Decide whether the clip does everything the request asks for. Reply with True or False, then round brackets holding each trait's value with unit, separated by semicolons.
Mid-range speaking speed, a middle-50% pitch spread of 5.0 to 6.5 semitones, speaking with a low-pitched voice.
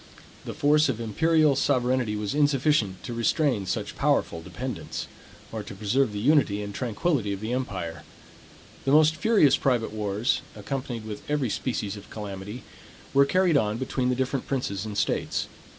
True (160 wpm; 5.3 semitones; 125 Hz)